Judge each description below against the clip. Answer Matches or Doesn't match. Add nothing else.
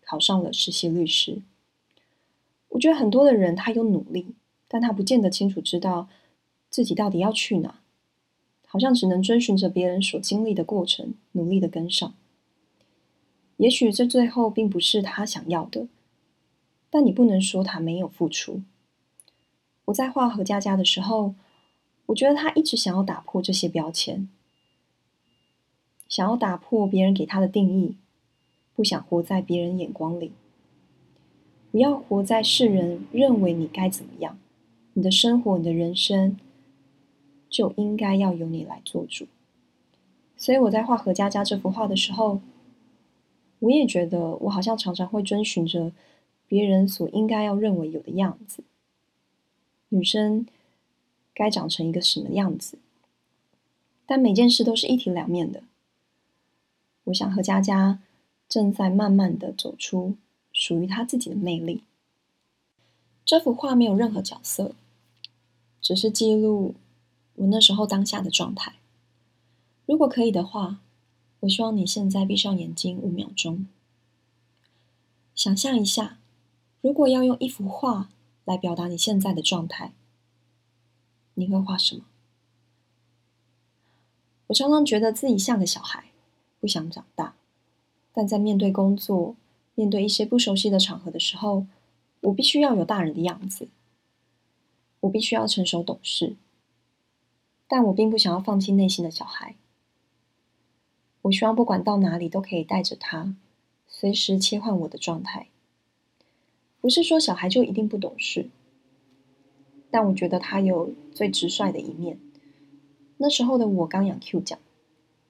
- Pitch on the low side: Doesn't match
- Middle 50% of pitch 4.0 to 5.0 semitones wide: Matches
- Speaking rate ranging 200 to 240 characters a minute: Matches